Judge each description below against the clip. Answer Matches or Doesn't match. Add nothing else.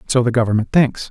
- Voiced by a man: Matches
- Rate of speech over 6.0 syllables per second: Matches